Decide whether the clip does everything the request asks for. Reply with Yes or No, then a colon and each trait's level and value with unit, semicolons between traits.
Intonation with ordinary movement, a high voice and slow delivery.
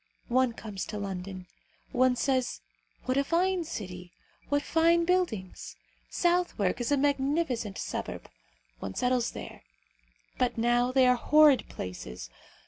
No: wide, 6.1 semitones; very high, 250 Hz; slow, 130 wpm